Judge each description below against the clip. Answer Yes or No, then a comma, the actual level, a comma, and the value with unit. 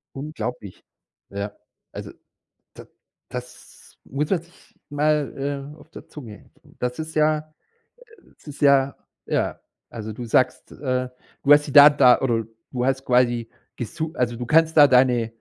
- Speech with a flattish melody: No, average, 3.3 semitones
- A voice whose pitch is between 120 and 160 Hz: Yes, low, 135 Hz